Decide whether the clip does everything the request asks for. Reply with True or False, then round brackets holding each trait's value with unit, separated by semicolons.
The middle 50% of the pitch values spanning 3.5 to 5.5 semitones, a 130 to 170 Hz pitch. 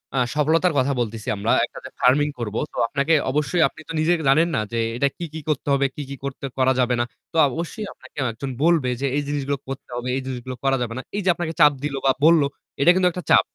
True (3.8 semitones; 140 Hz)